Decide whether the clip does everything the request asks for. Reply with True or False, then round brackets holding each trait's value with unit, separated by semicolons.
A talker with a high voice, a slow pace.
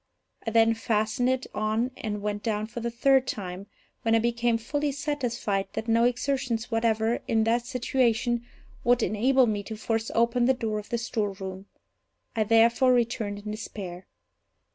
False (225 Hz; 165 wpm)